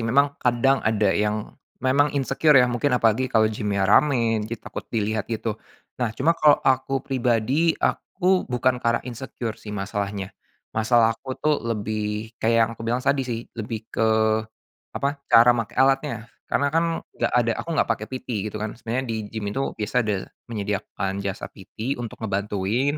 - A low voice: Yes, low, 115 Hz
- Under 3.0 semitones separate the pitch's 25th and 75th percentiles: No, average, 3.6 semitones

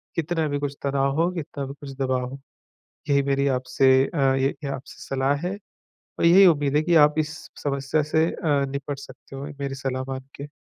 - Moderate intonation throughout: No, narrow, 1.8 semitones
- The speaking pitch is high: No, medium, 140 Hz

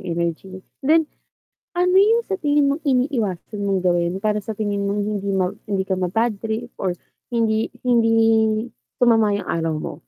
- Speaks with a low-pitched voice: No, high, 210 Hz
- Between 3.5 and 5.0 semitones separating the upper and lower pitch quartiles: Yes, average, 4.5 semitones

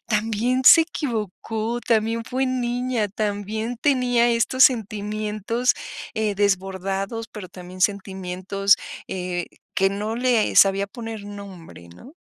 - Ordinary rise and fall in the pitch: Yes, average, 3.3 semitones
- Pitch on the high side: Yes, high, 215 Hz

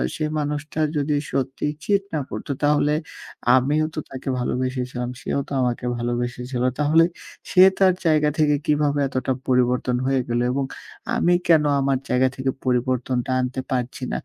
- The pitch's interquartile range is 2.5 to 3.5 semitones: Yes, average, 2.9 semitones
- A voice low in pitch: Yes, low, 130 Hz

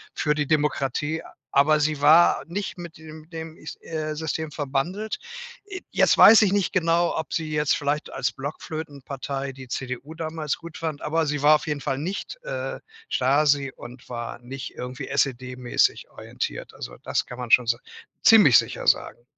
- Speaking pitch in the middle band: Yes, medium, 150 Hz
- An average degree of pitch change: Yes, average, 3.0 semitones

